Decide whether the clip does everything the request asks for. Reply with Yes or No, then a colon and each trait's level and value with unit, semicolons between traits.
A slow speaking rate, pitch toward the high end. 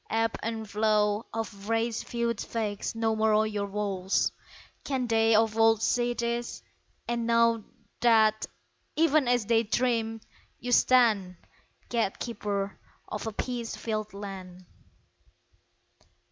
Yes: slow, 120 wpm; high, 225 Hz